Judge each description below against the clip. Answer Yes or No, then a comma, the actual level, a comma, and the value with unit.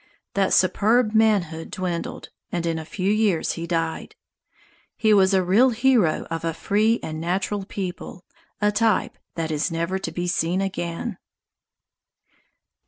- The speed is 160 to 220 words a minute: No, average, 145 wpm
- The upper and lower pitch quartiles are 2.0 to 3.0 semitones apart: No, average, 3.9 semitones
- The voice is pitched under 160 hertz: No, medium, 185 Hz